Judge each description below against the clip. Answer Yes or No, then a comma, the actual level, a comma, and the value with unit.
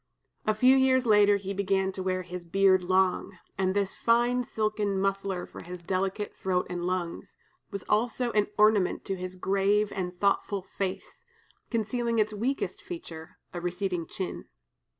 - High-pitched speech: Yes, high, 195 Hz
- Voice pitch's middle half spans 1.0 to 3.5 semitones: Yes, narrow, 2.5 semitones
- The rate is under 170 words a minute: Yes, average, 155 wpm